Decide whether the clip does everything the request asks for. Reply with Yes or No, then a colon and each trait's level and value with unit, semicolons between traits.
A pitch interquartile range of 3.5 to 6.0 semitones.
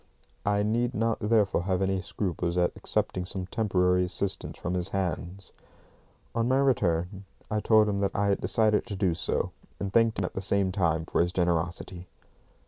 No: average, 2.8 semitones